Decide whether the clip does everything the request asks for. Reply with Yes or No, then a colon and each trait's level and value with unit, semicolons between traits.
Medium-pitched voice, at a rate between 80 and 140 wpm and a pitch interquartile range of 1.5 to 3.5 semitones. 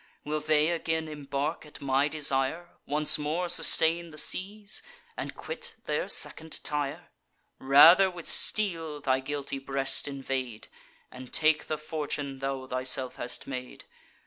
Yes: medium, 150 Hz; slow, 135 wpm; average, 3.1 semitones